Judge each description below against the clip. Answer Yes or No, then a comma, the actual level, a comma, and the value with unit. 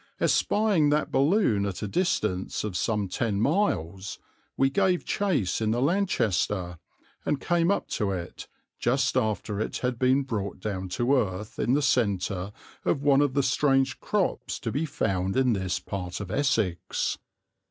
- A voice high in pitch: No, low, 115 Hz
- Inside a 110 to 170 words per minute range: Yes, average, 160 wpm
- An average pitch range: No, wide, 6.5 semitones